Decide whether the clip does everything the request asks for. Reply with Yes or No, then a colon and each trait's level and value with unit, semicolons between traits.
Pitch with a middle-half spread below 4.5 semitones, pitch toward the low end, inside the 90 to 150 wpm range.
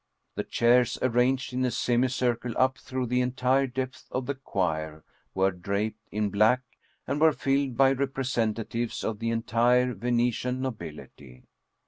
Yes: average, 2.9 semitones; low, 125 Hz; average, 140 wpm